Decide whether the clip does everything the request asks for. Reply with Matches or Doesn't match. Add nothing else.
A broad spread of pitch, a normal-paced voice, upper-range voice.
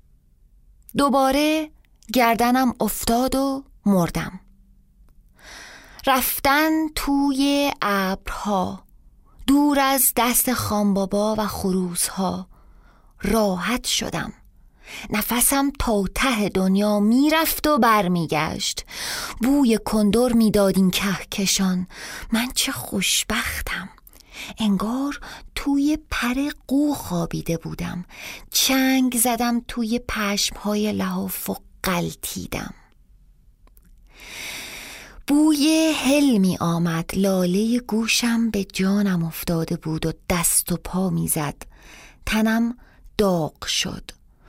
Doesn't match